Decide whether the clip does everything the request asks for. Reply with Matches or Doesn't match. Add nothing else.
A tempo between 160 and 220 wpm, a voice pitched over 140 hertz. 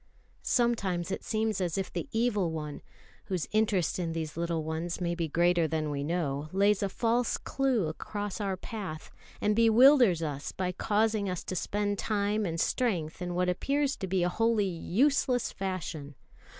Matches